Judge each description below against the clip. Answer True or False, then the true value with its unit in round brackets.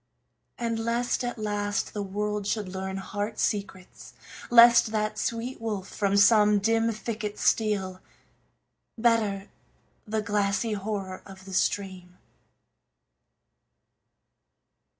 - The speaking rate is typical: False (105 wpm)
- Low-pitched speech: False (210 Hz)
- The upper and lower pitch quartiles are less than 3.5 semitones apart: True (2.4 semitones)